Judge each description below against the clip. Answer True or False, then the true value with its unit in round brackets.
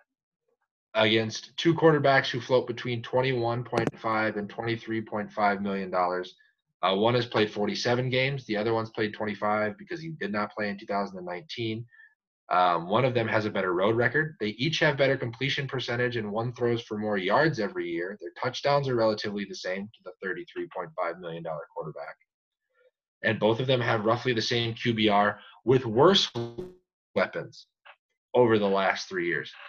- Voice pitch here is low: True (115 Hz)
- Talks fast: False (165 wpm)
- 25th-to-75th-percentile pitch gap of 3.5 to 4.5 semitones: True (3.8 semitones)